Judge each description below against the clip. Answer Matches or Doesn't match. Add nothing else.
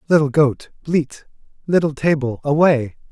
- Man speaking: Matches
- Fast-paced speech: Doesn't match